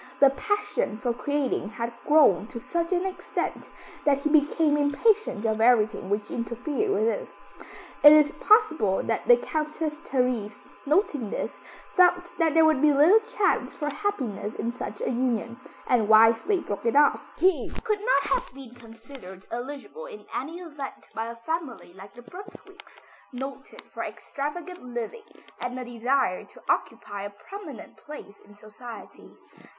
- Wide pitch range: Yes, wide, 6.5 semitones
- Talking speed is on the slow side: No, average, 155 wpm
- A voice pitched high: Yes, very high, 275 Hz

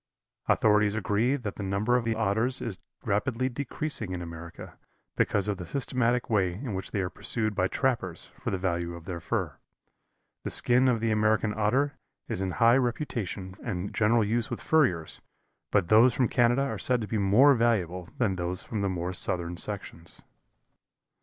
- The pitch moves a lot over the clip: No, average, 4.6 semitones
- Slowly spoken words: No, average, 180 wpm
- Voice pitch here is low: Yes, low, 105 Hz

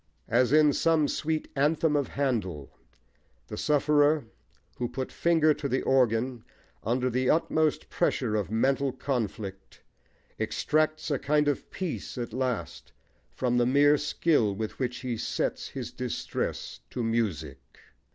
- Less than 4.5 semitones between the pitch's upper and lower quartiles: Yes, average, 4.1 semitones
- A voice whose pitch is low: Yes, low, 130 Hz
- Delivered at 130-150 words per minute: Yes, slow, 135 wpm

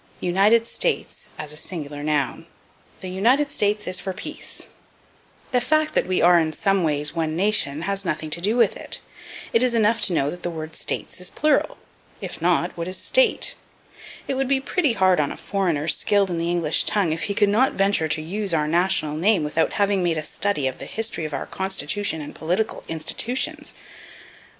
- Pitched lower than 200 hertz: Yes, medium, 185 Hz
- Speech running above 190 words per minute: Yes, average, 200 wpm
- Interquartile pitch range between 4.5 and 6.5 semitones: Yes, average, 4.9 semitones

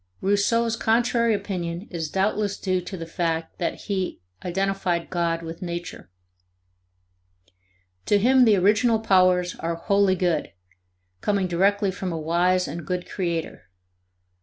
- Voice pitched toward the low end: No, medium, 185 Hz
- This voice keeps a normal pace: No, slow, 130 wpm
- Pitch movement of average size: Yes, average, 3.0 semitones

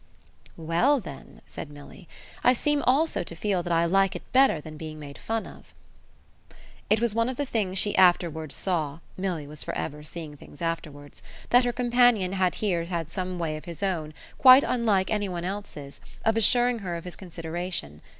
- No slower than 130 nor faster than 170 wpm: No, average, 190 wpm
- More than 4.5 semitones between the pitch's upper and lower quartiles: Yes, wide, 5.6 semitones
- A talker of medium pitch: Yes, medium, 180 Hz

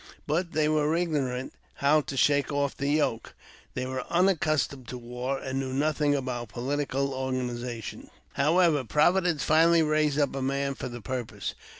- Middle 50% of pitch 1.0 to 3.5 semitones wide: Yes, average, 2.9 semitones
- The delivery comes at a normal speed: Yes, average, 160 wpm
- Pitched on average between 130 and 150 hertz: Yes, medium, 140 Hz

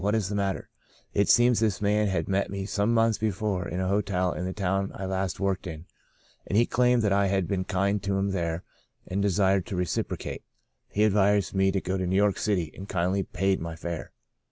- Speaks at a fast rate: Yes, fast, 225 wpm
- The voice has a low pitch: Yes, very low, 95 Hz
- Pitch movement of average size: No, narrow, 1.7 semitones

